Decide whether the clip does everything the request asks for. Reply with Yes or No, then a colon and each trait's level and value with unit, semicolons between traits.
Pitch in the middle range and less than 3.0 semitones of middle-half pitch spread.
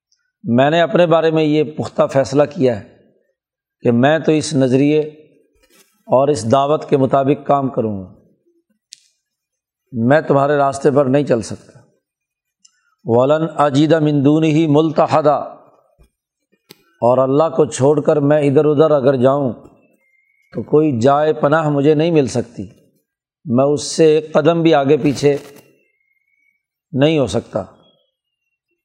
Yes: medium, 150 Hz; narrow, 2.6 semitones